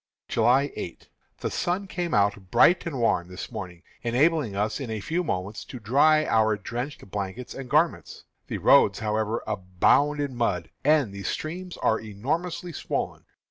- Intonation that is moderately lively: No, wide, 7.0 semitones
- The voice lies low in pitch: Yes, low, 120 Hz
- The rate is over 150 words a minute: Yes, average, 160 wpm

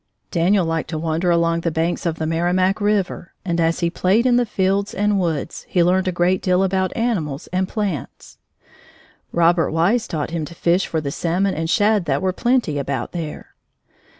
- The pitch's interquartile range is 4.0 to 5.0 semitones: No, average, 2.9 semitones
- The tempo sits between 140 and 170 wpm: No, average, 190 wpm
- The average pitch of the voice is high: No, medium, 175 Hz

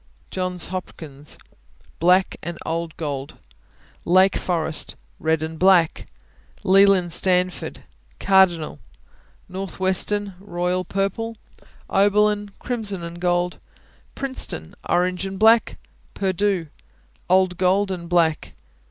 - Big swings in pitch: No, narrow, 2.4 semitones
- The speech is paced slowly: Yes, slow, 95 wpm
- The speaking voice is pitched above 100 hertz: Yes, medium, 185 Hz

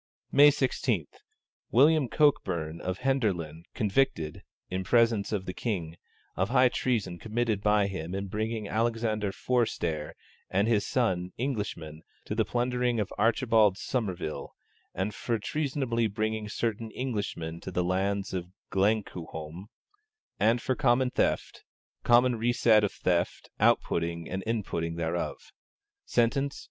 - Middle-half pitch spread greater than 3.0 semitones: Yes, average, 4.6 semitones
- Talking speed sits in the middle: No, slow, 130 wpm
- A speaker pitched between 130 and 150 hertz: No, low, 105 Hz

